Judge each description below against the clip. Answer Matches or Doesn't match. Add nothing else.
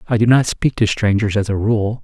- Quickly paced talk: Matches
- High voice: Doesn't match